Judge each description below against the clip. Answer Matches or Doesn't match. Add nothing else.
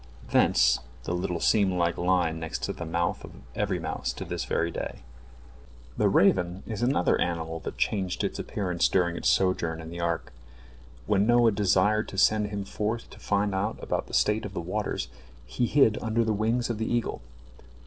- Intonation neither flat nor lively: Matches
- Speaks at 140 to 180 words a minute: Doesn't match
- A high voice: Doesn't match